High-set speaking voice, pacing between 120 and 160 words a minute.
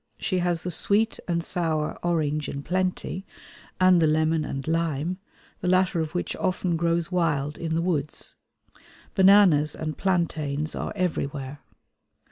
No: medium, 165 Hz; average, 140 wpm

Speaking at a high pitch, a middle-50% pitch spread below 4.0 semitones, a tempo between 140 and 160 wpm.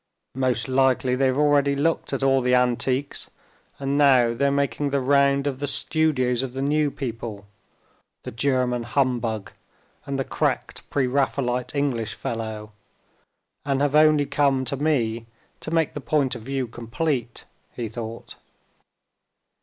No: low, 135 Hz; average, 2.7 semitones; average, 145 wpm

